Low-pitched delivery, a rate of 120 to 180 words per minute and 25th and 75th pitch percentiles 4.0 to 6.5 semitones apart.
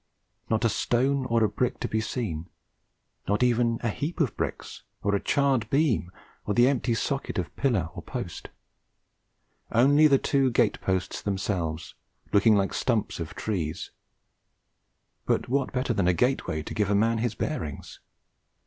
Yes: low, 115 Hz; average, 165 wpm; average, 4.4 semitones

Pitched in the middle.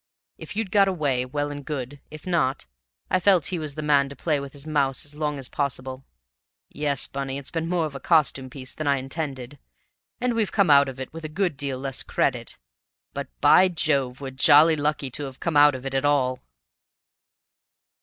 Yes: medium, 145 Hz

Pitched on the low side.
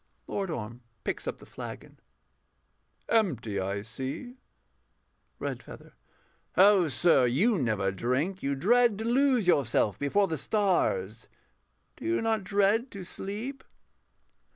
No: high, 190 Hz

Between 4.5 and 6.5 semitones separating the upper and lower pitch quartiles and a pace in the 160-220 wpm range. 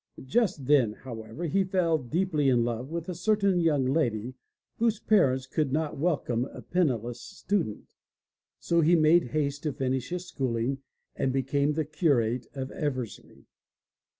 No: average, 4.9 semitones; average, 150 wpm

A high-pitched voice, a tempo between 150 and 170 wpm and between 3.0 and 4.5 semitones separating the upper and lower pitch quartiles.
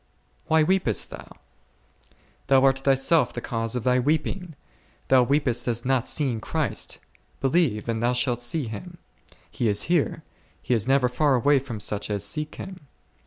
No: low, 130 Hz; average, 165 wpm; average, 4.0 semitones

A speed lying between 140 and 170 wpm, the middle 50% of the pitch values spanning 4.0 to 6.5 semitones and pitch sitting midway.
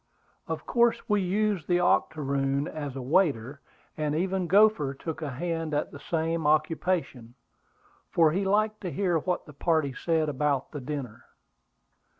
Yes: average, 150 wpm; average, 4.3 semitones; medium, 160 Hz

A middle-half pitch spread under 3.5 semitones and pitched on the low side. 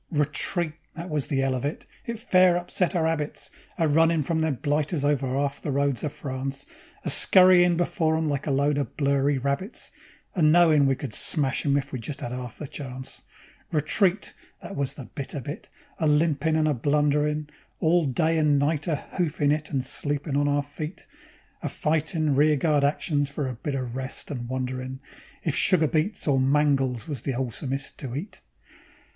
No: narrow, 2.6 semitones; medium, 145 Hz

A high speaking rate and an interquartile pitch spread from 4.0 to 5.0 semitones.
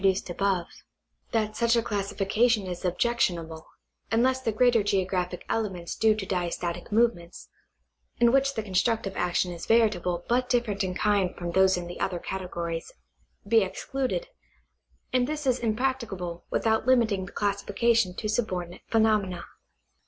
No: average, 145 wpm; average, 4.5 semitones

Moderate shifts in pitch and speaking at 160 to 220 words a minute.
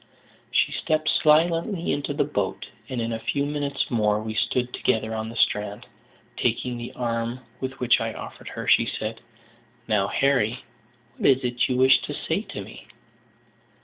Yes: average, 4.0 semitones; average, 165 wpm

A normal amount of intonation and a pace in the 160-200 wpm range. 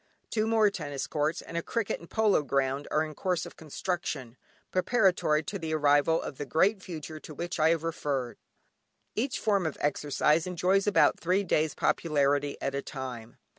Yes: average, 4.3 semitones; average, 175 wpm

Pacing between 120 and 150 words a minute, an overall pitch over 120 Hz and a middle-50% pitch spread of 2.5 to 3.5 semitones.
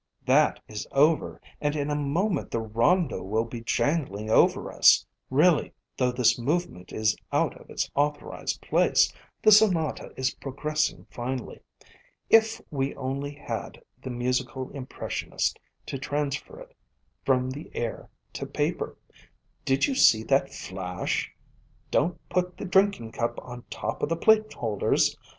No: average, 140 wpm; low, 135 Hz; average, 5.3 semitones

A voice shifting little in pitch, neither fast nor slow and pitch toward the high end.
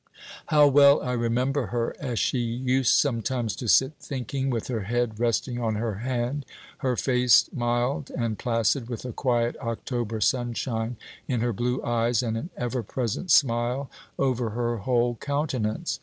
No: narrow, 2.1 semitones; average, 155 wpm; low, 120 Hz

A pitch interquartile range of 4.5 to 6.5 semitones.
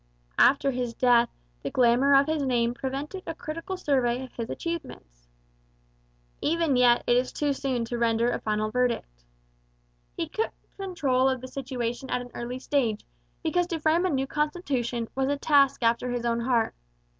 No: average, 3.5 semitones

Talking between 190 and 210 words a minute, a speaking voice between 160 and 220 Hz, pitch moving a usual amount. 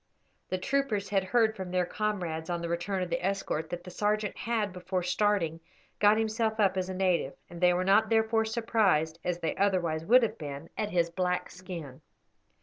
Yes: average, 195 wpm; medium, 185 Hz; average, 3.6 semitones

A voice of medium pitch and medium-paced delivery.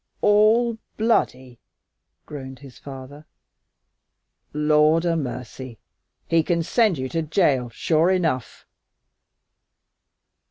No: medium, 155 Hz; slow, 90 wpm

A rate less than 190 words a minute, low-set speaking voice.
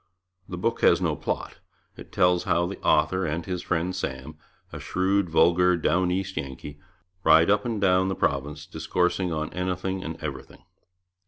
Yes: average, 165 wpm; very low, 90 Hz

